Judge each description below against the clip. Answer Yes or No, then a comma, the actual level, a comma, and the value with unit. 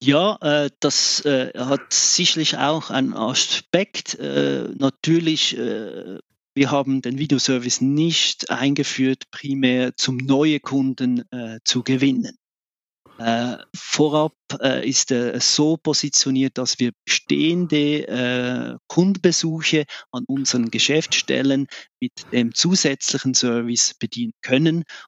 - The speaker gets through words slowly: Yes, slow, 90 wpm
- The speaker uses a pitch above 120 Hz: Yes, low, 135 Hz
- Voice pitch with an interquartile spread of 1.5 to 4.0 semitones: Yes, average, 3.6 semitones